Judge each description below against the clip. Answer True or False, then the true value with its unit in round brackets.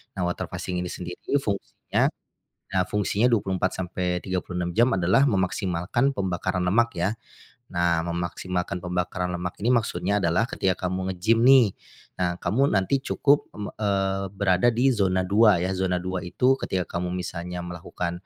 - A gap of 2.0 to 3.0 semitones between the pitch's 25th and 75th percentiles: True (2.6 semitones)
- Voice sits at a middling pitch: False (95 Hz)